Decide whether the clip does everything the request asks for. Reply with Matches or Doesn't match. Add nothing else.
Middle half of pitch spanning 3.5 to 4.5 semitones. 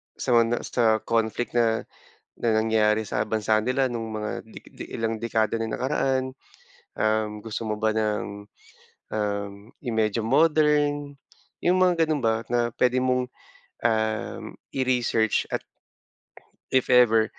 Doesn't match